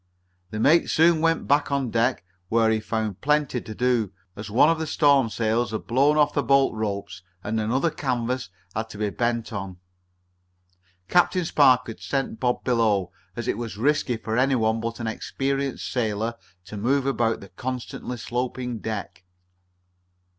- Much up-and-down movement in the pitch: No, average, 3.7 semitones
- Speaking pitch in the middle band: No, low, 120 Hz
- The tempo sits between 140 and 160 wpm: No, average, 170 wpm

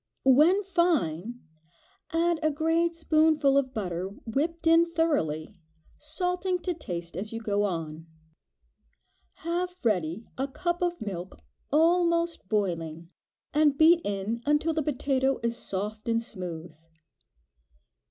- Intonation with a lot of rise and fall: Yes, wide, 9.0 semitones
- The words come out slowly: Yes, slow, 120 wpm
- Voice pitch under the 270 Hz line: No, very high, 275 Hz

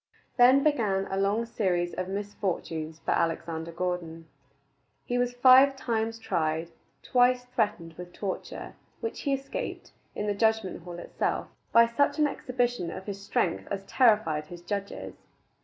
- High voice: Yes, high, 205 Hz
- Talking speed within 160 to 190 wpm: No, average, 150 wpm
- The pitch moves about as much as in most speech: No, wide, 5.9 semitones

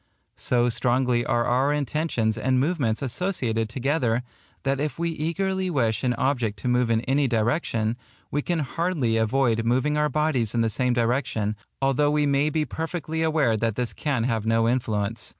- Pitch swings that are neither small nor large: Yes, average, 4.6 semitones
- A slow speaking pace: No, average, 170 wpm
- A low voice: Yes, low, 130 Hz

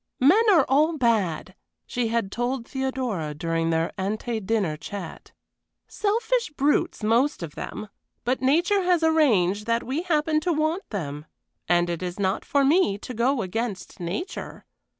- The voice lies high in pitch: Yes, high, 235 Hz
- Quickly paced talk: No, average, 150 wpm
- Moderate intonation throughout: No, wide, 8.4 semitones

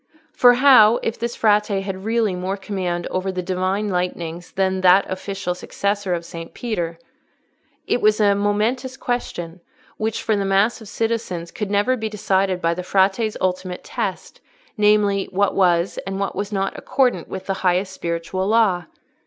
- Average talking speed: Yes, average, 165 wpm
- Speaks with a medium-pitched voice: No, high, 195 Hz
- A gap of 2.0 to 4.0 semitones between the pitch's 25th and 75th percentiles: Yes, narrow, 2.6 semitones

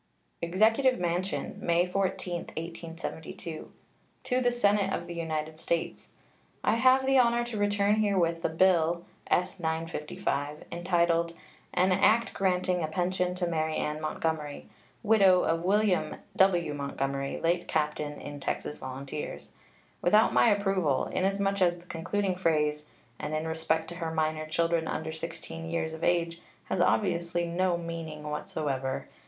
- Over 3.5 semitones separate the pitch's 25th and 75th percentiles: No, average, 3.0 semitones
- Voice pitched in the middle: Yes, medium, 170 Hz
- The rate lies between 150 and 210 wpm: No, average, 140 wpm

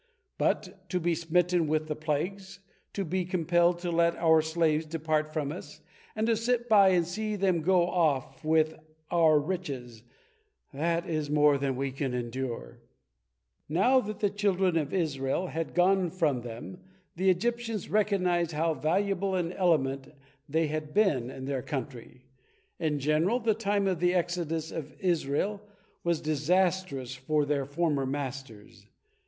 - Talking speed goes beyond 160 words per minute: No, average, 150 wpm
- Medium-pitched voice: Yes, medium, 165 Hz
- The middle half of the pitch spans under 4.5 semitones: Yes, average, 4.0 semitones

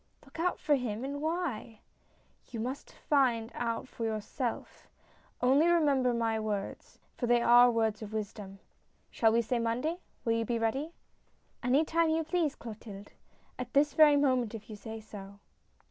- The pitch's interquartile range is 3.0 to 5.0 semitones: Yes, average, 4.4 semitones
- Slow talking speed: No, average, 175 wpm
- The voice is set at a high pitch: Yes, high, 240 Hz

